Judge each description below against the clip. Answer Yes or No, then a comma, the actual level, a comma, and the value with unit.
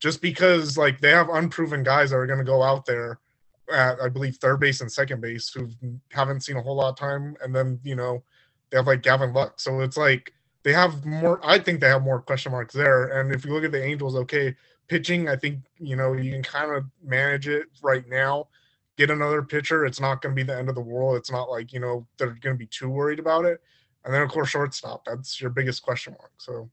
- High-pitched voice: No, low, 135 Hz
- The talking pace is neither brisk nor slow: No, fast, 250 wpm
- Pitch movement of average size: No, narrow, 2.1 semitones